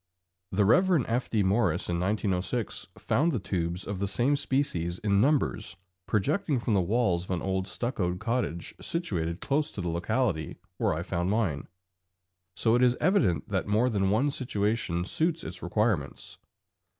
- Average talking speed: Yes, average, 160 wpm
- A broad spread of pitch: Yes, wide, 5.8 semitones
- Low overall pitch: Yes, low, 105 Hz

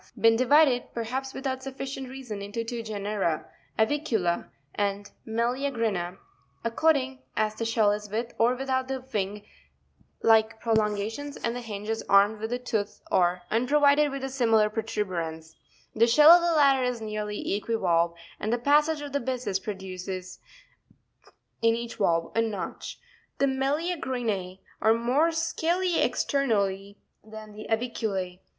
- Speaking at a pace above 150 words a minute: No, average, 145 wpm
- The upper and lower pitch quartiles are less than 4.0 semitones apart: No, average, 4.4 semitones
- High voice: Yes, high, 225 Hz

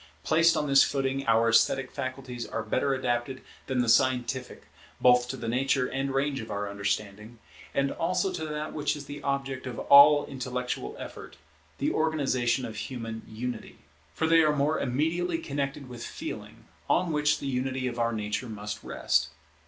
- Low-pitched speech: Yes, low, 130 Hz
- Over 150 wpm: Yes, average, 170 wpm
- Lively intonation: No, average, 3.2 semitones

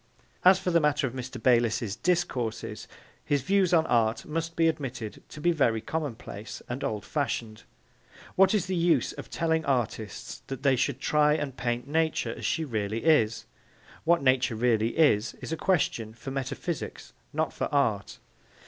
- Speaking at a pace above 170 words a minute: No, average, 165 wpm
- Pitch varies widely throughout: Yes, wide, 5.7 semitones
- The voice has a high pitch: No, low, 135 Hz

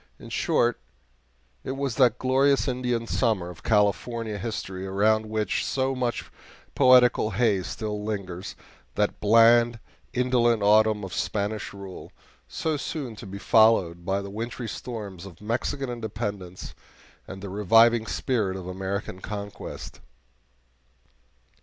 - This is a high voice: No, low, 110 Hz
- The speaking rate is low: Yes, slow, 125 wpm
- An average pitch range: Yes, average, 3.3 semitones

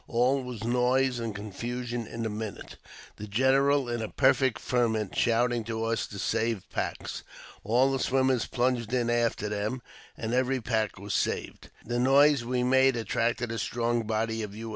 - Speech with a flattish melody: Yes, narrow, 2.2 semitones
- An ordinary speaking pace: Yes, average, 170 wpm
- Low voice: Yes, low, 120 Hz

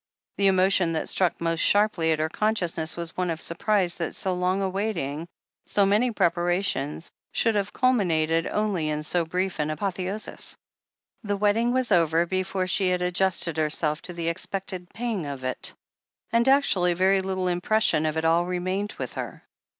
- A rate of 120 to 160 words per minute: No, average, 175 wpm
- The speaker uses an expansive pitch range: No, average, 3.2 semitones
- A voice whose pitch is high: No, medium, 180 Hz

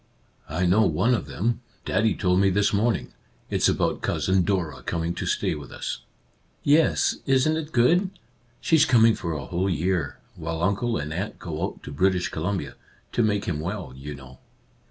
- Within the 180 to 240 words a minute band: Yes, average, 190 wpm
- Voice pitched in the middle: No, very low, 95 Hz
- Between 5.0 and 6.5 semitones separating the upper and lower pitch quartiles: Yes, wide, 5.6 semitones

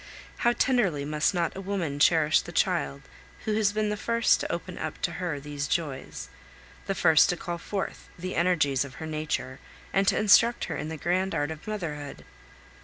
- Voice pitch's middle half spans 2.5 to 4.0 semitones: No, average, 5.0 semitones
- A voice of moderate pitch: Yes, medium, 170 Hz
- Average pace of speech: Yes, average, 190 wpm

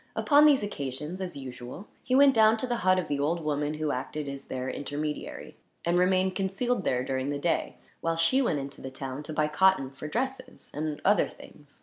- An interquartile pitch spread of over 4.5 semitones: Yes, wide, 5.4 semitones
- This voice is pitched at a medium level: Yes, medium, 155 Hz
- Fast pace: Yes, fast, 210 wpm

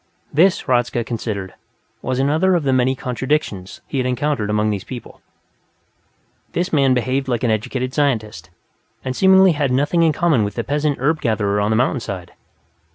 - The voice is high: No, low, 130 Hz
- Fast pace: No, average, 165 wpm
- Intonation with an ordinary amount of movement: Yes, average, 4.7 semitones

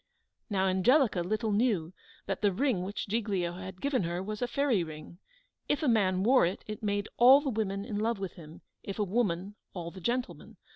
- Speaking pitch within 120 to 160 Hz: No, high, 205 Hz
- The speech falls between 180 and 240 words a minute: Yes, average, 200 wpm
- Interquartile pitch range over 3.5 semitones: Yes, average, 4.2 semitones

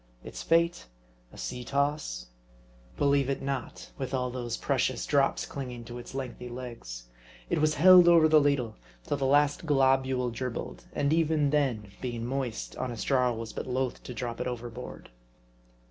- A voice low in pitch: Yes, low, 130 Hz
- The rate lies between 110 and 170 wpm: Yes, average, 160 wpm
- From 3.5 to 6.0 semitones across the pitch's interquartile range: No, average, 2.9 semitones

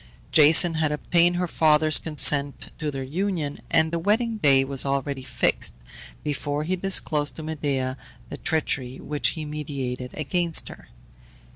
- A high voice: No, medium, 150 Hz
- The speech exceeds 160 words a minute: No, average, 145 wpm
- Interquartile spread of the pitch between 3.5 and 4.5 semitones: No, average, 2.9 semitones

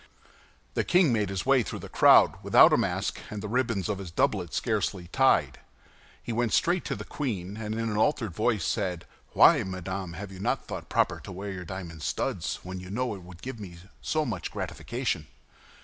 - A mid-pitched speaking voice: No, low, 100 Hz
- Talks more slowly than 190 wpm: No, average, 200 wpm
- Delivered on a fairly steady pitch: No, average, 4.3 semitones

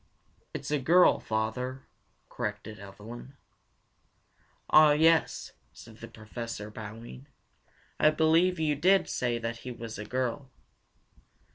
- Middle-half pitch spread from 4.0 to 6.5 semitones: Yes, wide, 5.5 semitones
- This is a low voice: Yes, low, 120 Hz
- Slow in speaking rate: Yes, slow, 115 wpm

